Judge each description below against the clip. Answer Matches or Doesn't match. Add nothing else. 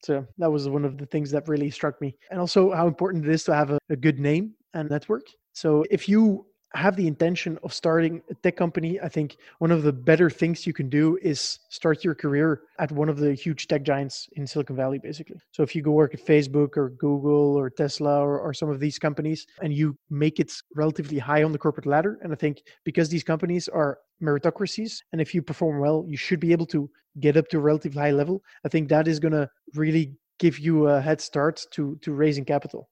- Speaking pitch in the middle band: Matches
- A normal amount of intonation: Doesn't match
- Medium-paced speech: Doesn't match